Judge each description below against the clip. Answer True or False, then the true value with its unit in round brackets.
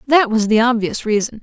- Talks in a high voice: True (230 Hz)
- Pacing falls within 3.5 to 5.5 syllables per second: True (5.3 syllables/s)